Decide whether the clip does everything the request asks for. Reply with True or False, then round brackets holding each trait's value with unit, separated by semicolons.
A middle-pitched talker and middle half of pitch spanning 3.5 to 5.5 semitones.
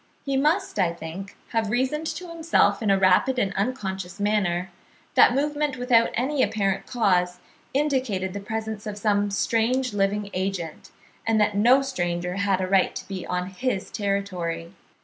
False (205 Hz; 5.1 semitones)